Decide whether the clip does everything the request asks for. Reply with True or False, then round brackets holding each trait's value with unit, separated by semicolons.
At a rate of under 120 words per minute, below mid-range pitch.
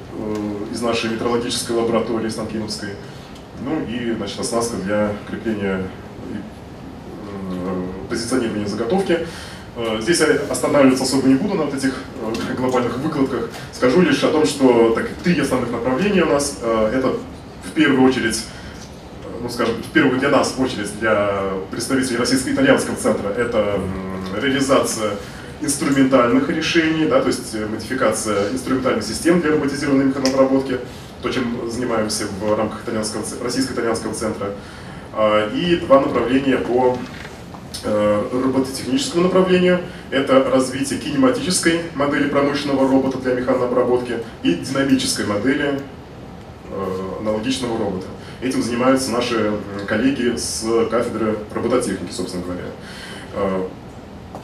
True (110 wpm; 120 Hz)